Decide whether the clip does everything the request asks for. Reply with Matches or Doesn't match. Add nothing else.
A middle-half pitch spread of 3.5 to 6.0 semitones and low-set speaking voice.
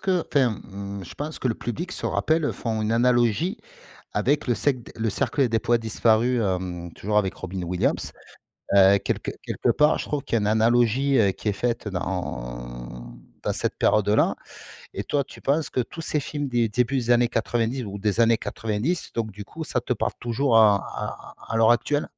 Matches